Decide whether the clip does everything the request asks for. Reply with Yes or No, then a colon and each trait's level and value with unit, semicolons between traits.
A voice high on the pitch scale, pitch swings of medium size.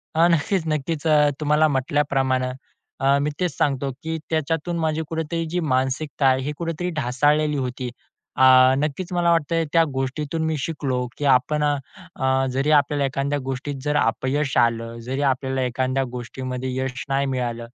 No: medium, 145 Hz; average, 3.0 semitones